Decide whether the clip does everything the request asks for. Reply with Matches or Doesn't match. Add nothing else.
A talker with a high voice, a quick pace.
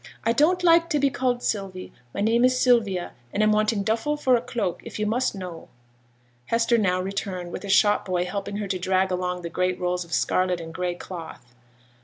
Matches